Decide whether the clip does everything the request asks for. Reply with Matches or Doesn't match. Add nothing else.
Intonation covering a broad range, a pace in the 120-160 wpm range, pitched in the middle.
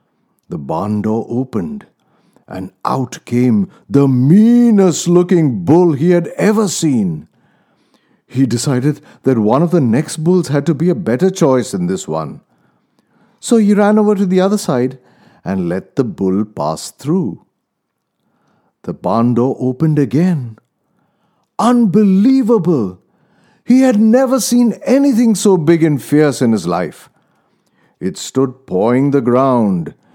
Matches